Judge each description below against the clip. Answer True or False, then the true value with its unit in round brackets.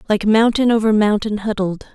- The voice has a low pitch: False (215 Hz)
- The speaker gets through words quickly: False (155 wpm)